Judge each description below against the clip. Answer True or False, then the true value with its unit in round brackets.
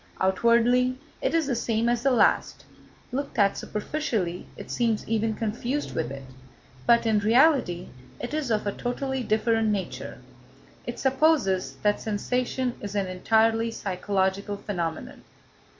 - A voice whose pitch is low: False (225 Hz)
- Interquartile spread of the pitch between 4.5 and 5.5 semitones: False (3.6 semitones)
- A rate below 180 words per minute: True (135 wpm)